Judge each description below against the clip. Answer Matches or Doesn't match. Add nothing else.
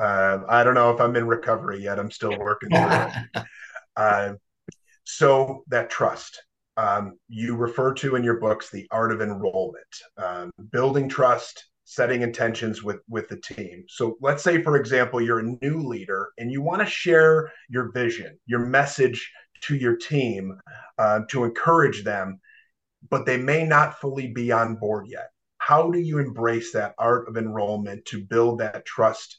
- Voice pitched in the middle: Doesn't match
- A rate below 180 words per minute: Matches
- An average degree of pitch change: Matches